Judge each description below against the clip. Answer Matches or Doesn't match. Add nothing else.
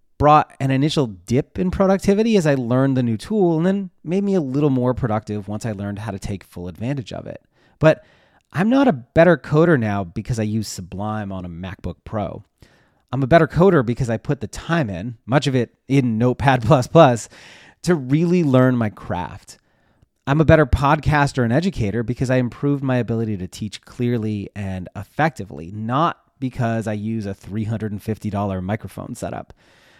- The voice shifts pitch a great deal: Matches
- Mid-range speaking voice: Doesn't match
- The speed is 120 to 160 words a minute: Doesn't match